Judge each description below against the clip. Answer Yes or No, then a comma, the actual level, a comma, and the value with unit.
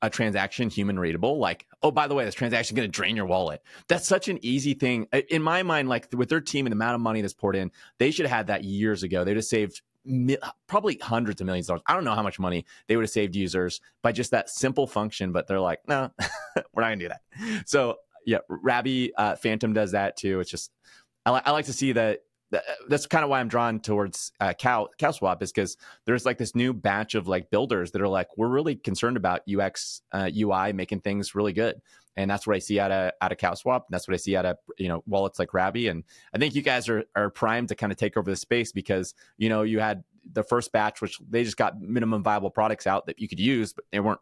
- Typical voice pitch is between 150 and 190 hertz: No, low, 110 Hz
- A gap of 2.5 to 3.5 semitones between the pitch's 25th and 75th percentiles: No, average, 4.2 semitones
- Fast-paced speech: Yes, fast, 255 wpm